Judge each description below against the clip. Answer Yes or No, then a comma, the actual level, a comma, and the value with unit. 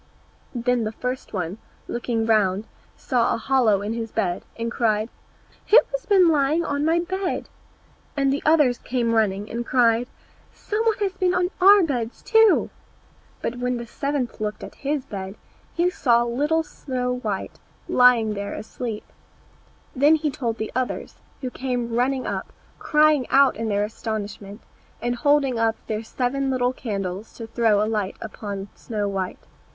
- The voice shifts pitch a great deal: No, average, 4.4 semitones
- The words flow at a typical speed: Yes, average, 160 wpm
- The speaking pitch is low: No, high, 240 Hz